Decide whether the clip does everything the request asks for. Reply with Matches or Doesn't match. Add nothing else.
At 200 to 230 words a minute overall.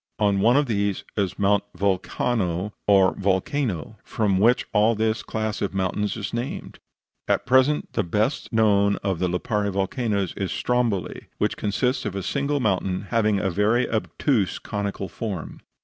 Doesn't match